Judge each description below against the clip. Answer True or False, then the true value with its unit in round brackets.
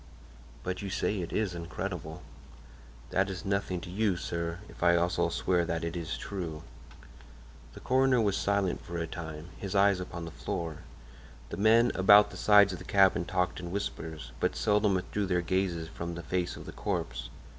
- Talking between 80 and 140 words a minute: False (185 wpm)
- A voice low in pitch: True (90 Hz)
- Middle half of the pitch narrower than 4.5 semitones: True (2.8 semitones)